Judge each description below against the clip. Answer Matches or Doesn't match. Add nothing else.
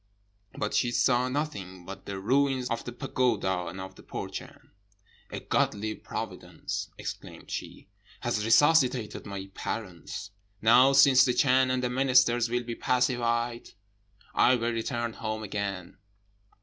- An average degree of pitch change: Matches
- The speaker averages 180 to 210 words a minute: Doesn't match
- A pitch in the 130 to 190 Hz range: Doesn't match